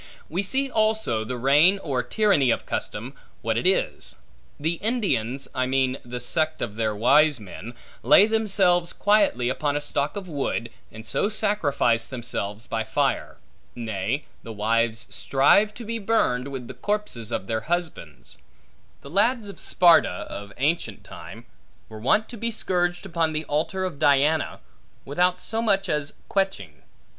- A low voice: No, medium, 150 Hz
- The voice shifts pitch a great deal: Yes, wide, 8.6 semitones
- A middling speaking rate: Yes, average, 155 wpm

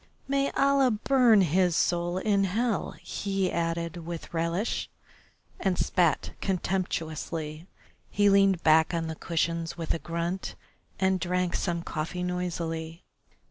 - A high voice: No, medium, 175 Hz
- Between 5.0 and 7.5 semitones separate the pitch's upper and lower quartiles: No, narrow, 2.6 semitones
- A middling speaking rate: No, slow, 125 wpm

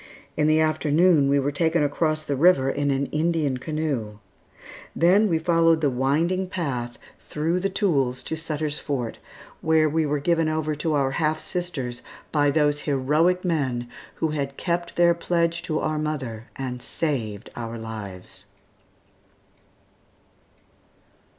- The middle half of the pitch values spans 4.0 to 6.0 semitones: No, average, 3.4 semitones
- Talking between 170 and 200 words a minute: No, average, 140 wpm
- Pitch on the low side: No, medium, 150 Hz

